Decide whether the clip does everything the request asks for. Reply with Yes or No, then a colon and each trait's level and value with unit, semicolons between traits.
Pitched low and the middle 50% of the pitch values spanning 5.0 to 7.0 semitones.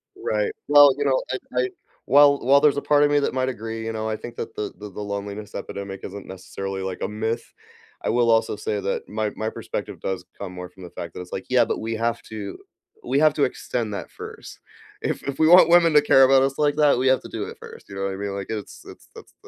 Yes: low, 115 Hz; average, 5.3 semitones